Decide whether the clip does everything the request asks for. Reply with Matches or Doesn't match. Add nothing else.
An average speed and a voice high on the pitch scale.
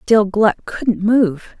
Matches